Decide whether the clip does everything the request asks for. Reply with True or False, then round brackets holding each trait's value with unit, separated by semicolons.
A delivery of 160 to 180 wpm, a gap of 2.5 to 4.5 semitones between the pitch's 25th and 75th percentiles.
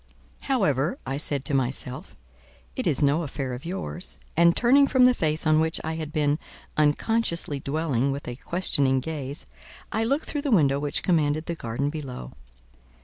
True (170 wpm; 3.7 semitones)